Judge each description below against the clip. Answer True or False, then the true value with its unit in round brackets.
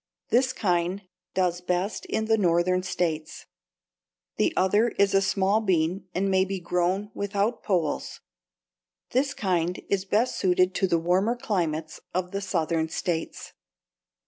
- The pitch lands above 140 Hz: True (185 Hz)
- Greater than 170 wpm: False (140 wpm)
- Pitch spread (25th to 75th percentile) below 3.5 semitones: True (2.5 semitones)